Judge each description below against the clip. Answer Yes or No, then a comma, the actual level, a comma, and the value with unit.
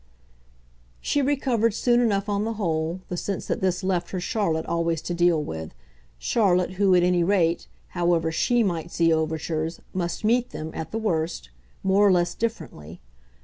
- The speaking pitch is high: No, medium, 180 Hz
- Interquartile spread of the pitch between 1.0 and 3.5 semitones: No, average, 3.9 semitones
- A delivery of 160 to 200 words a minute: Yes, average, 170 wpm